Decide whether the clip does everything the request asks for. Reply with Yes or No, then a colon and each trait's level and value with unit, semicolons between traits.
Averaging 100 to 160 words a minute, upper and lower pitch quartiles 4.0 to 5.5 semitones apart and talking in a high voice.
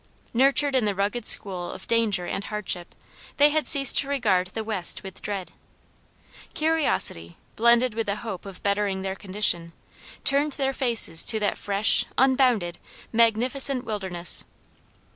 Yes: average, 145 wpm; average, 5.2 semitones; high, 215 Hz